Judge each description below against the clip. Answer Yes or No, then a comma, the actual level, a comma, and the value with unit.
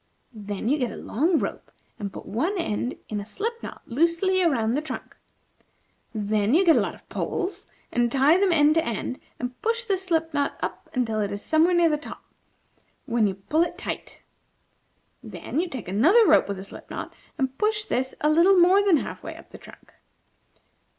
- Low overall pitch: No, very high, 300 Hz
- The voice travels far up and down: Yes, wide, 7.7 semitones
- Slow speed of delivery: No, average, 195 wpm